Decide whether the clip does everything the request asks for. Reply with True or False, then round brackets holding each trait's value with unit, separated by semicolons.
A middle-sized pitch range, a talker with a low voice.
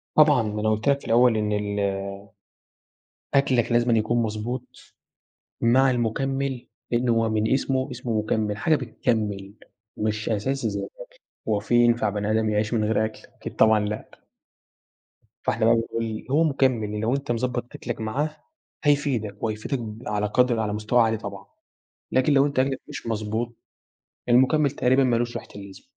True (3.2 semitones; 115 Hz)